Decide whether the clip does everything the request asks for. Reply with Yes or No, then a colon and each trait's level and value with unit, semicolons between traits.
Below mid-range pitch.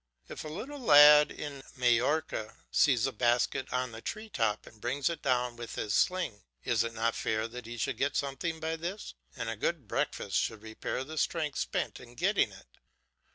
Yes: low, 130 Hz